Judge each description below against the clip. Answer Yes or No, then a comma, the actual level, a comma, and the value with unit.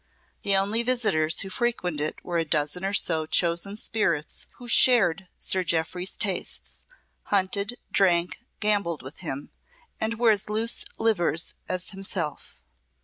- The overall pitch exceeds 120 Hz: Yes, high, 190 Hz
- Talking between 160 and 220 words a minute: No, average, 140 wpm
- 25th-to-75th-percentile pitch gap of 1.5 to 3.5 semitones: No, average, 4.1 semitones